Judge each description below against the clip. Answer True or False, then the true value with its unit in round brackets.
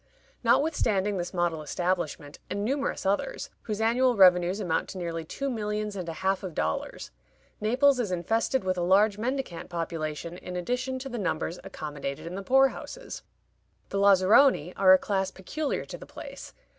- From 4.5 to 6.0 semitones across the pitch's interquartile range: True (5.2 semitones)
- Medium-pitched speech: False (195 Hz)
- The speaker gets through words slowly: False (170 wpm)